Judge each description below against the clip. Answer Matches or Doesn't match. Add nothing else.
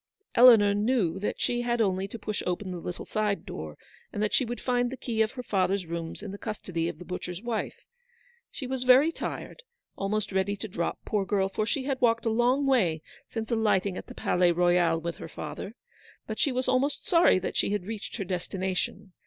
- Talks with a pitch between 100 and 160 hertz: Doesn't match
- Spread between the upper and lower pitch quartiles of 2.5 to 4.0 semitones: Doesn't match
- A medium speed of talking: Doesn't match